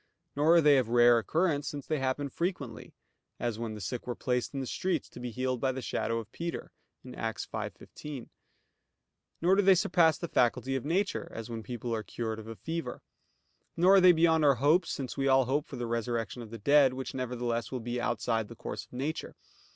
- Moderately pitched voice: No, low, 130 Hz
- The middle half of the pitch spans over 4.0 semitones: Yes, average, 4.7 semitones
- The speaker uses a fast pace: Yes, fast, 215 wpm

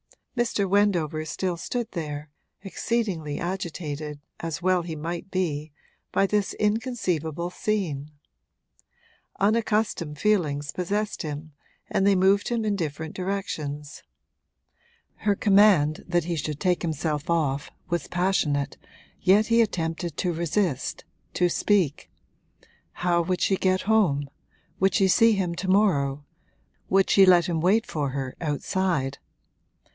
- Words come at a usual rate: No, slow, 125 wpm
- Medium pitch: Yes, medium, 175 Hz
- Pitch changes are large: No, average, 4.5 semitones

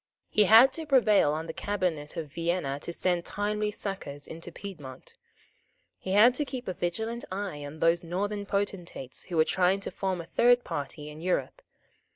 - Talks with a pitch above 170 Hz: Yes, medium, 185 Hz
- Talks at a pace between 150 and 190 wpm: Yes, average, 180 wpm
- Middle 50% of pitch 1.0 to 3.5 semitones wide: No, average, 4.4 semitones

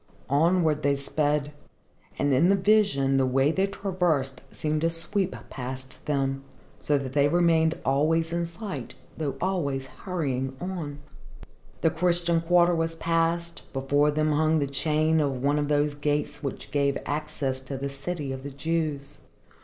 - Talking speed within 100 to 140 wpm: No, average, 155 wpm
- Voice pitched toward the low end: No, medium, 150 Hz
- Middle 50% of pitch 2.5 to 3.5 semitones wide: Yes, average, 3.2 semitones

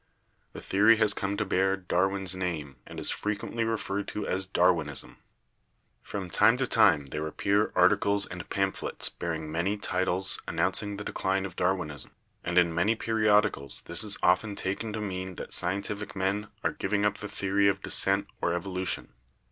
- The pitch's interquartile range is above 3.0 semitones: No, narrow, 2.5 semitones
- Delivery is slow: No, average, 170 wpm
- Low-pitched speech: Yes, very low, 95 Hz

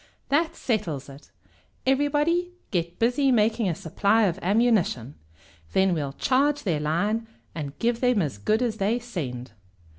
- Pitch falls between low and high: No, high, 210 Hz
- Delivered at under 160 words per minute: Yes, average, 145 wpm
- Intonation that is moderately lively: No, wide, 7.0 semitones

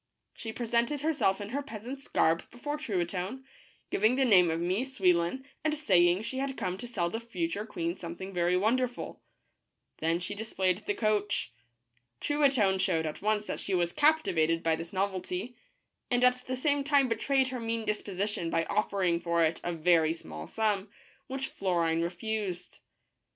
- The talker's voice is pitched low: No, high, 200 Hz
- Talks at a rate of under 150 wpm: No, average, 170 wpm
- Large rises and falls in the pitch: Yes, wide, 6.2 semitones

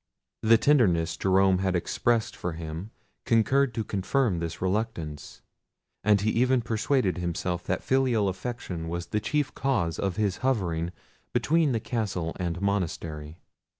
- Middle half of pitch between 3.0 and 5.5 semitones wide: Yes, average, 5.2 semitones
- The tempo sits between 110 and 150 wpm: Yes, average, 140 wpm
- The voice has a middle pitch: No, very low, 95 Hz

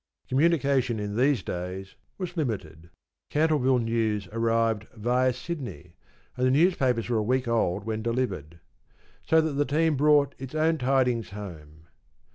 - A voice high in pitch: No, low, 125 Hz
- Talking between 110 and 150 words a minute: Yes, average, 140 wpm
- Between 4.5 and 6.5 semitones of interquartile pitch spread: Yes, average, 5.2 semitones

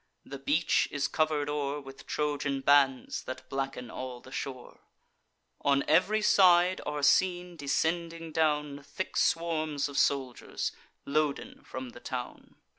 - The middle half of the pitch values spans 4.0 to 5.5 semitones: No, average, 2.9 semitones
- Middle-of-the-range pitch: Yes, medium, 145 Hz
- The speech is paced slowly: Yes, slow, 130 wpm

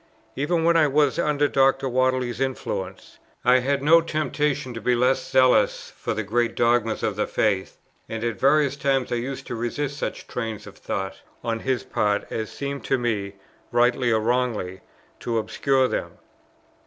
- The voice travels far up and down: No, average, 3.4 semitones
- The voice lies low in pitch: Yes, low, 125 Hz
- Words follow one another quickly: No, average, 170 wpm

